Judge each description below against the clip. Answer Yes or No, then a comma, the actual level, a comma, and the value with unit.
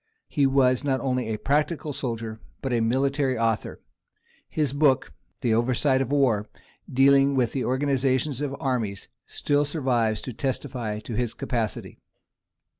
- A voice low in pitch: Yes, low, 130 Hz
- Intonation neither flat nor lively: Yes, average, 3.0 semitones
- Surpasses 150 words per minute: No, slow, 135 wpm